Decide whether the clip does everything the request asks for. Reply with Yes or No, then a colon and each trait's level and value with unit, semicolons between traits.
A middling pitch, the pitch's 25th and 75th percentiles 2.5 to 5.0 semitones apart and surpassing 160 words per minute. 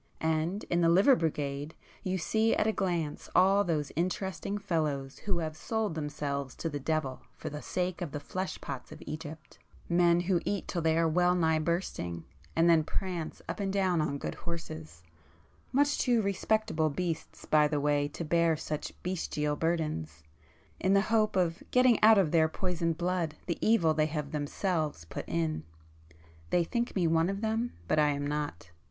Yes: medium, 165 Hz; average, 3.8 semitones; average, 175 wpm